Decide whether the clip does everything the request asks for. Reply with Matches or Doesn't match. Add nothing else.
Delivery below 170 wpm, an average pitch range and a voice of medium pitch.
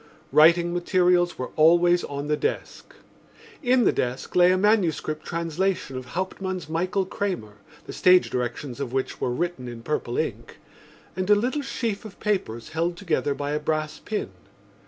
Matches